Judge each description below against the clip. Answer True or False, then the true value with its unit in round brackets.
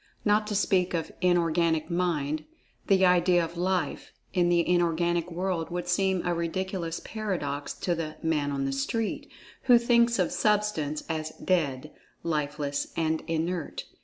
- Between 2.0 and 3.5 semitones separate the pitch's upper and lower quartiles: True (3.0 semitones)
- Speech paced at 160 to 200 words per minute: False (145 wpm)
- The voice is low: False (175 Hz)